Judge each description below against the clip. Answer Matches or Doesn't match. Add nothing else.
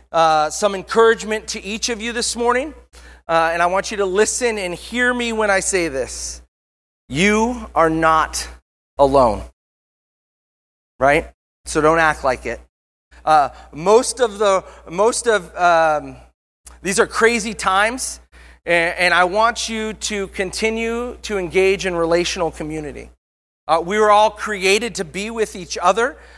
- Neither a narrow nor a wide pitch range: Doesn't match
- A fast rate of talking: Doesn't match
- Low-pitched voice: Doesn't match